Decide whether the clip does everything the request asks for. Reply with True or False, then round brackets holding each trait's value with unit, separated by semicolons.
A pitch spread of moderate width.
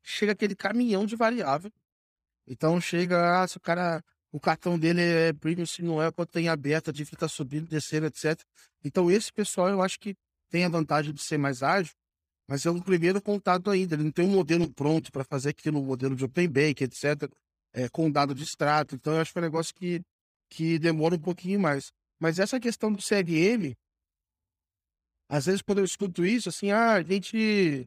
True (4.3 semitones)